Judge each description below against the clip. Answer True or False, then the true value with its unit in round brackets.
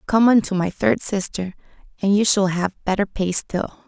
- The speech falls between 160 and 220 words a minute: True (200 wpm)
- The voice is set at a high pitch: True (200 Hz)